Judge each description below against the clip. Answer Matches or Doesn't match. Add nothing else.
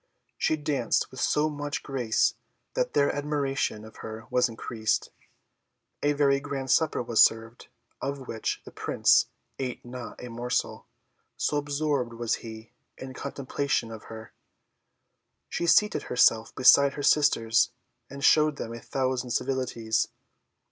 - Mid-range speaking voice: Doesn't match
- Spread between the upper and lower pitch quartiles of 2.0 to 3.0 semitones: Doesn't match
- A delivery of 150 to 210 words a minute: Doesn't match